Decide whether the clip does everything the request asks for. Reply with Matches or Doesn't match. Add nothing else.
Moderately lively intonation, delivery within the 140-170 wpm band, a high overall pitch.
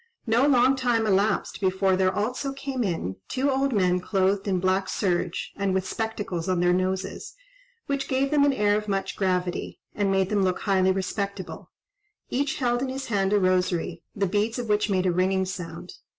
Doesn't match